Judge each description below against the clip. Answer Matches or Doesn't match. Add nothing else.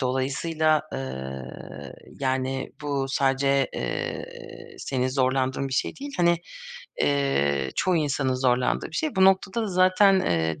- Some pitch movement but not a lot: Doesn't match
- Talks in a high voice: Doesn't match